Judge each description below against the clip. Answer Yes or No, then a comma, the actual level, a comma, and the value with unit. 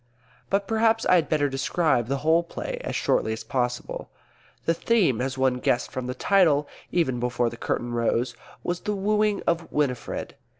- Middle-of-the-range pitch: Yes, medium, 145 Hz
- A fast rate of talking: No, average, 175 wpm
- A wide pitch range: Yes, wide, 6.4 semitones